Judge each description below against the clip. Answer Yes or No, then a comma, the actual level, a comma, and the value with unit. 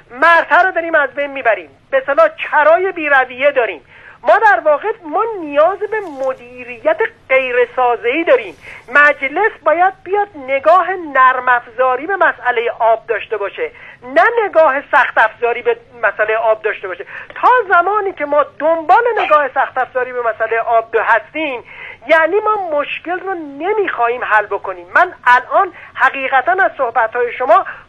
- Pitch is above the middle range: Yes, very high, 300 Hz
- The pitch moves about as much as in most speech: No, wide, 7.0 semitones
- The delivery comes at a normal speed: Yes, average, 145 wpm